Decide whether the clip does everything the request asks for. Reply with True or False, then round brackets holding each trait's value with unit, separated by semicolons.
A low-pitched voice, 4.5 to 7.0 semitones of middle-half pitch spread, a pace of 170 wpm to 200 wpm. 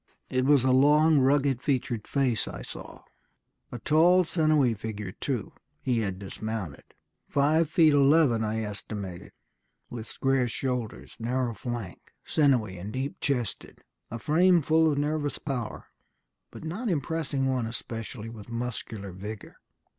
False (130 Hz; 4.8 semitones; 135 wpm)